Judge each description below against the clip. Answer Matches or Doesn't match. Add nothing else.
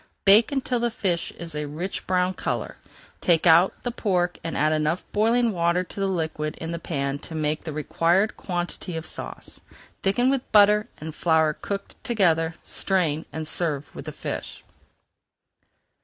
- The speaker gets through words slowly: Doesn't match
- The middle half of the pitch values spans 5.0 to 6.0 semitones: Doesn't match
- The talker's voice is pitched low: Doesn't match